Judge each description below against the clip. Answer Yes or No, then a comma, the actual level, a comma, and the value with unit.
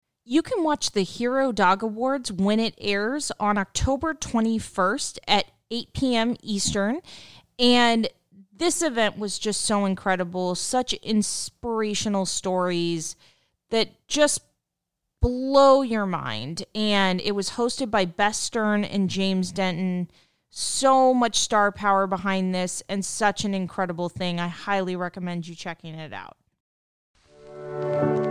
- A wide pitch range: No, average, 4.0 semitones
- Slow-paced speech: Yes, slow, 125 wpm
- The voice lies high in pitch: Yes, high, 200 Hz